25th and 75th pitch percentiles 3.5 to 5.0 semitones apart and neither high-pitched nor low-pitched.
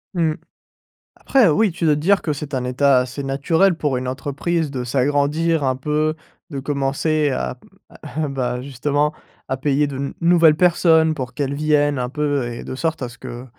No: average, 3.0 semitones; medium, 145 Hz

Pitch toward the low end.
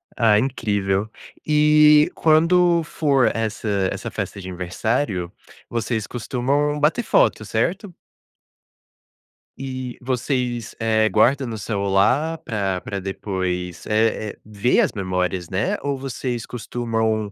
Yes: low, 115 Hz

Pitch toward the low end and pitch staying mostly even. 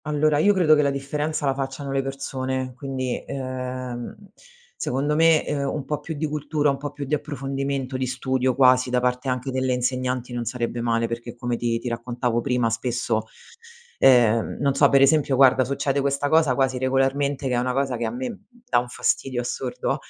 Yes: low, 130 Hz; narrow, 2.1 semitones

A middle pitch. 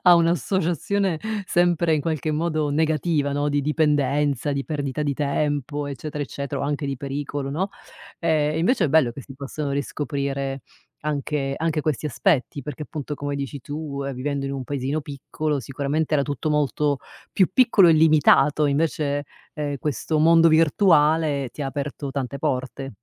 Yes: medium, 145 Hz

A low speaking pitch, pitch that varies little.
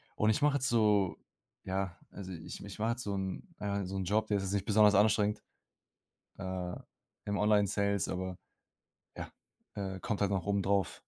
Yes: low, 100 Hz; narrow, 1.8 semitones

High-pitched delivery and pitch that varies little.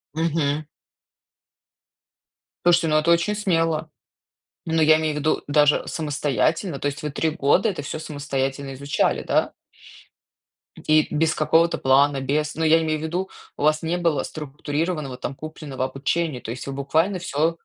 No: medium, 155 Hz; narrow, 2.3 semitones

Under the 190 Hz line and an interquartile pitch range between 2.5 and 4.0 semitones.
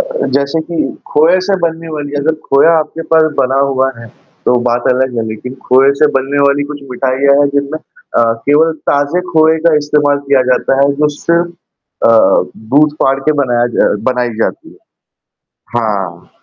Yes: medium, 140 Hz; average, 3.2 semitones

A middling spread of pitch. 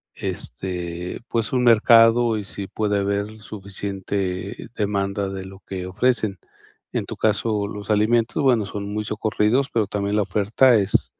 No: narrow, 2.1 semitones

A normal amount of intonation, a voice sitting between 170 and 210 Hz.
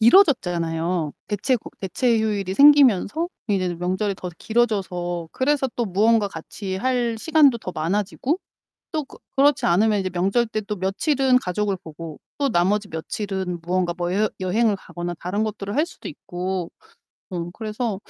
Yes: average, 5.0 semitones; high, 200 Hz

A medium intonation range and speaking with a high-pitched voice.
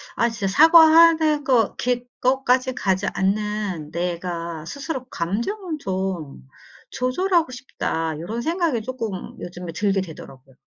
No: wide, 7.1 semitones; high, 220 Hz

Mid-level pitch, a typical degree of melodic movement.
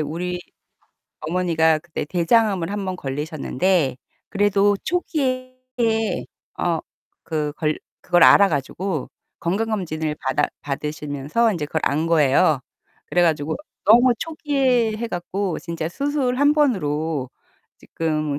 No: medium, 175 Hz; wide, 5.9 semitones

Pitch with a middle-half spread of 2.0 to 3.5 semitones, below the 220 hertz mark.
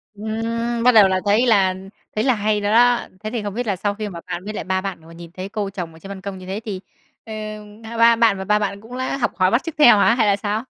Yes: average, 2.9 semitones; high, 210 Hz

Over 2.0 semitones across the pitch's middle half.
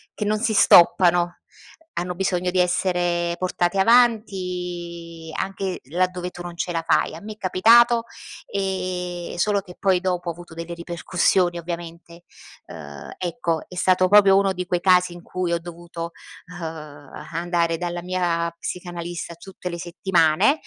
No: narrow, 1.5 semitones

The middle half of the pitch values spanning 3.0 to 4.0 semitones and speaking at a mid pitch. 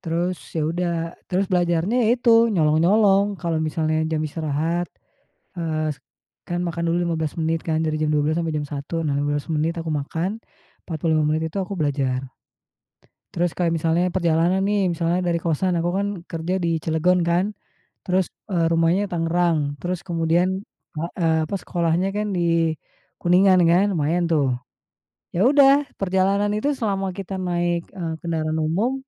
No: narrow, 2.4 semitones; medium, 170 Hz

